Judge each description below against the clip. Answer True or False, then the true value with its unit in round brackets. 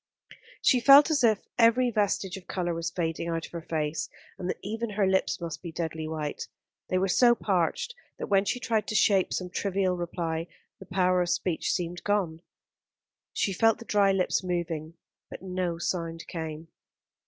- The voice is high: False (180 Hz)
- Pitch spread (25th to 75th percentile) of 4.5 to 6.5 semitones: False (3.5 semitones)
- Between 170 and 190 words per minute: True (180 wpm)